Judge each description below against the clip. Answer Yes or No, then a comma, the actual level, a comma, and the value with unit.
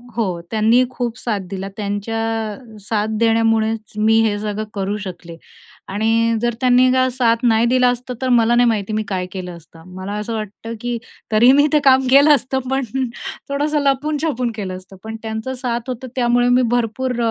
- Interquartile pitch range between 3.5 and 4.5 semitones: No, average, 2.9 semitones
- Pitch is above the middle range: Yes, high, 230 Hz